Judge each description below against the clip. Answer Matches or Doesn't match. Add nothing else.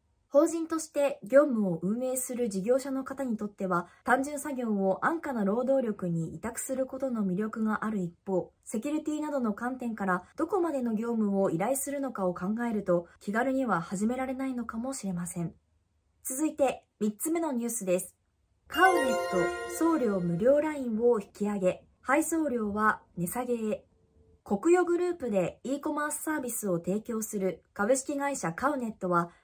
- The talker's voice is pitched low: Doesn't match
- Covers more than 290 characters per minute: Matches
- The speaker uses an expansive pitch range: Matches